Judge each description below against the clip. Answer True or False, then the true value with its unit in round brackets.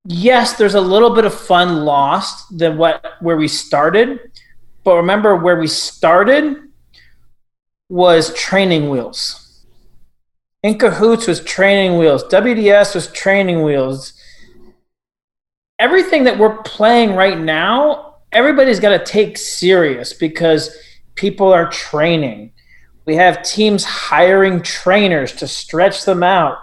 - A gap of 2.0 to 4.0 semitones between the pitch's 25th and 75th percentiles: False (4.8 semitones)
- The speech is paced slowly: True (120 wpm)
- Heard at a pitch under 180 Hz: False (185 Hz)